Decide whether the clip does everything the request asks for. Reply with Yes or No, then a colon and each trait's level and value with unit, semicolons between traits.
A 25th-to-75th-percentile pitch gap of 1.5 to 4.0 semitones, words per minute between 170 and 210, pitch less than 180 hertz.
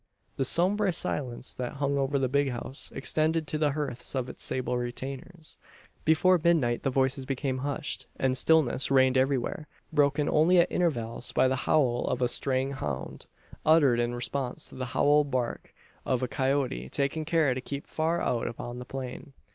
Yes: average, 3.1 semitones; average, 175 wpm; low, 135 Hz